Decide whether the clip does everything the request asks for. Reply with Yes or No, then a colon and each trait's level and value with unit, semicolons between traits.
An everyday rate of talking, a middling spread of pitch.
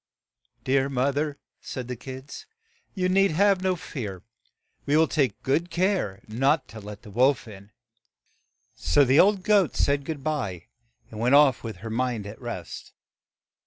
No: average, 160 wpm; wide, 5.7 semitones